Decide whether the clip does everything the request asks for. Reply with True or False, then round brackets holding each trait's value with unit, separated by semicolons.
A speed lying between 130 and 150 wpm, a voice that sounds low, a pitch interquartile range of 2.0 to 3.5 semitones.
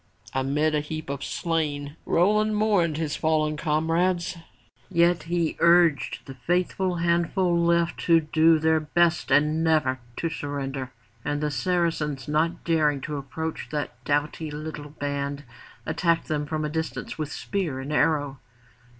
False (140 wpm; 155 Hz; 2.5 semitones)